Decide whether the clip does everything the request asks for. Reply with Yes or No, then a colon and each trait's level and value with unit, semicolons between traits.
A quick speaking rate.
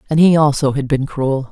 Yes: fast, 240 wpm